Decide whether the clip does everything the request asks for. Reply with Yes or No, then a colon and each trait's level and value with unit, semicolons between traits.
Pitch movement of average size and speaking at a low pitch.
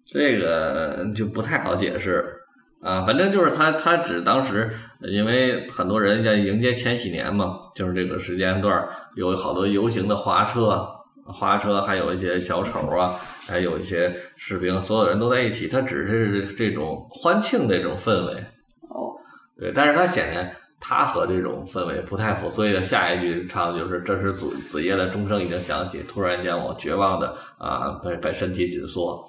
Yes: average, 4.2 semitones; low, 100 Hz